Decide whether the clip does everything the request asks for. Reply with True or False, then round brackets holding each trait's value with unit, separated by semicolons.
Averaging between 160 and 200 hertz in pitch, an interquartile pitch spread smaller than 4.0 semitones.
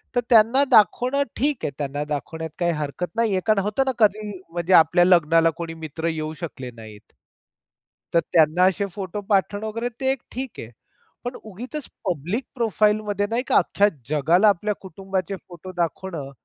False (190 Hz; 4.9 semitones)